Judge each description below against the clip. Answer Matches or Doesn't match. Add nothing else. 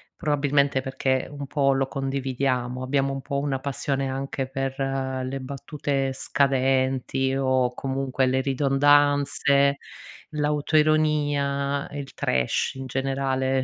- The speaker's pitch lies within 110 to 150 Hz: Matches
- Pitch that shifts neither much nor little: Doesn't match